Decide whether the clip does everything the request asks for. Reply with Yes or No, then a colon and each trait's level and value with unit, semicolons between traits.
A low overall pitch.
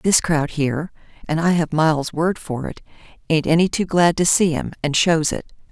No: medium, 160 Hz